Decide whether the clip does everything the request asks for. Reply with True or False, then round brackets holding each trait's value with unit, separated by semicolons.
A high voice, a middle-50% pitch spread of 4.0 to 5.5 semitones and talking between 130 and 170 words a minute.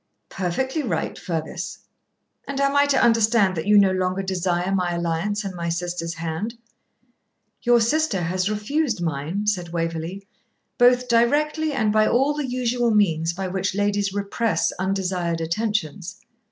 True (195 Hz; 5.2 semitones; 145 wpm)